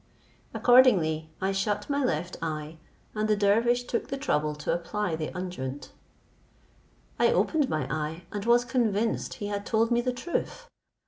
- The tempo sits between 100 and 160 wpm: Yes, average, 150 wpm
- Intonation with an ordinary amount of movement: No, wide, 7.0 semitones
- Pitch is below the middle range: No, high, 205 Hz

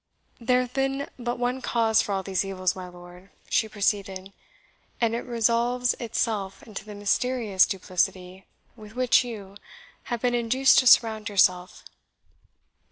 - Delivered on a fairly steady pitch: No, average, 4.0 semitones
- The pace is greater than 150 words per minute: No, average, 145 wpm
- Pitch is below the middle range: No, high, 220 Hz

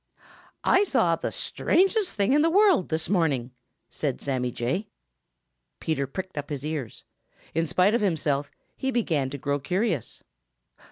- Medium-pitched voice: Yes, medium, 165 Hz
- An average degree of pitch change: No, wide, 7.3 semitones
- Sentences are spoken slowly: No, average, 150 wpm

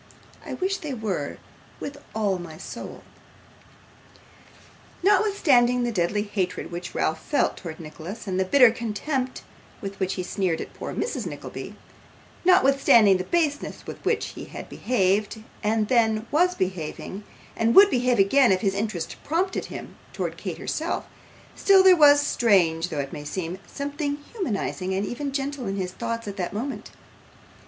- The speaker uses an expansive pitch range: Yes, wide, 6.8 semitones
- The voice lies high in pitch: Yes, high, 220 Hz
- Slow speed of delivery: No, average, 155 wpm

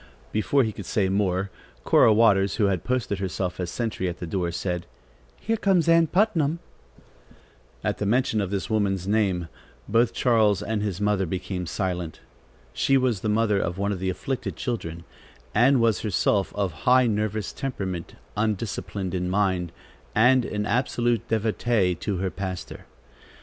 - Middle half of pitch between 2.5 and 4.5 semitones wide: Yes, average, 3.8 semitones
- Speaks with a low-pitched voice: Yes, low, 105 Hz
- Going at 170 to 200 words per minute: No, average, 160 wpm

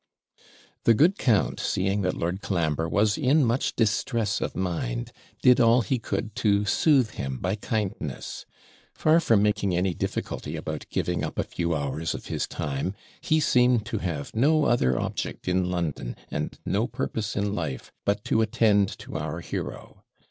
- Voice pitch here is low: Yes, low, 100 Hz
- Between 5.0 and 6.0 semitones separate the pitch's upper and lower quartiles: Yes, wide, 5.5 semitones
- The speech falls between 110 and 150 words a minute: No, average, 165 wpm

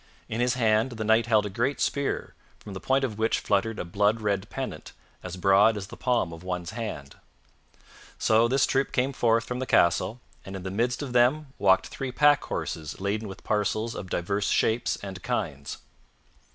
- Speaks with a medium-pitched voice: No, low, 110 Hz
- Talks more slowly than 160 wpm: No, average, 190 wpm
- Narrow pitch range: No, average, 4.1 semitones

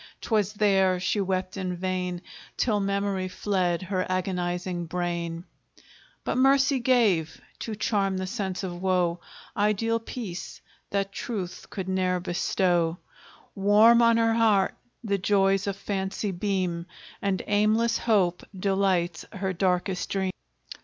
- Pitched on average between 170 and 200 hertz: Yes, high, 190 Hz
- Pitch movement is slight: Yes, narrow, 2.3 semitones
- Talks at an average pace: No, slow, 125 wpm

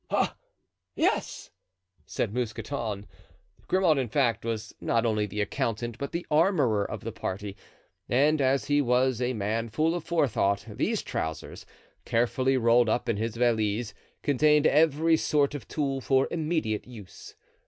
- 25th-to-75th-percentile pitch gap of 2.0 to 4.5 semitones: No, average, 4.9 semitones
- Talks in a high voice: No, low, 120 Hz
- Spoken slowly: No, average, 145 wpm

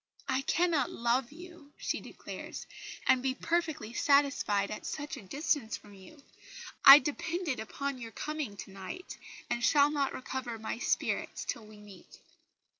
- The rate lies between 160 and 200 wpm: No, average, 150 wpm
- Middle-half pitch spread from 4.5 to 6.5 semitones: Yes, average, 5.1 semitones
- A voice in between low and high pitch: No, very high, 270 Hz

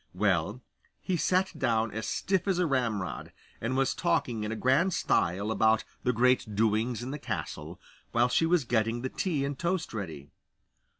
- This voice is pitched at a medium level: No, low, 125 Hz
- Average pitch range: No, wide, 6.3 semitones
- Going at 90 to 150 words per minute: No, average, 175 wpm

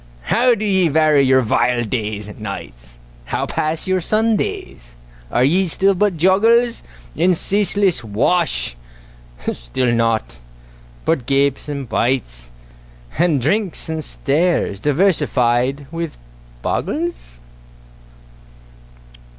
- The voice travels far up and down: Yes, wide, 8.0 semitones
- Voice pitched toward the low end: No, medium, 150 Hz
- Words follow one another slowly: Yes, slow, 105 wpm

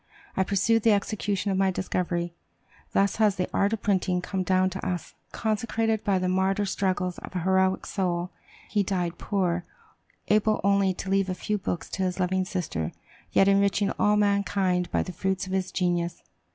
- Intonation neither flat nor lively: No, narrow, 1.7 semitones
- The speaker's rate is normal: Yes, average, 180 wpm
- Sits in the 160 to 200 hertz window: Yes, high, 190 Hz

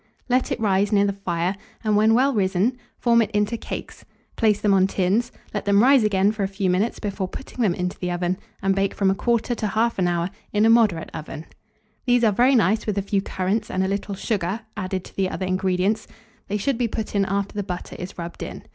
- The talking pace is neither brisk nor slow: No, fast, 225 wpm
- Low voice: No, high, 200 Hz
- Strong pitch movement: No, average, 2.8 semitones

